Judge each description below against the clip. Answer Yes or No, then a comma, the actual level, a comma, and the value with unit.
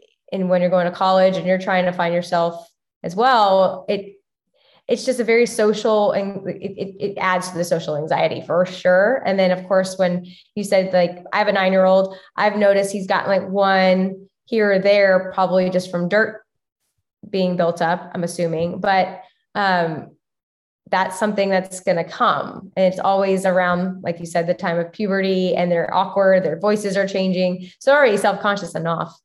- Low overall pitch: No, high, 190 Hz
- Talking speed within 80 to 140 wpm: No, average, 195 wpm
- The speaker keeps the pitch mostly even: Yes, narrow, 1.7 semitones